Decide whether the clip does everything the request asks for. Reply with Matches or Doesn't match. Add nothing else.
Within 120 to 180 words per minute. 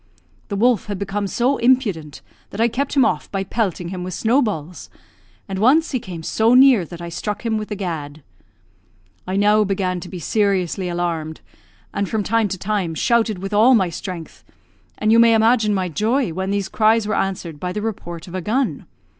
Doesn't match